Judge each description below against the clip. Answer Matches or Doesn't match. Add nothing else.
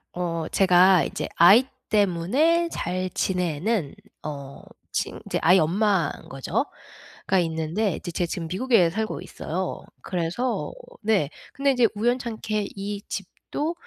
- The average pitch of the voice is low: Doesn't match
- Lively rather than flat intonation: Doesn't match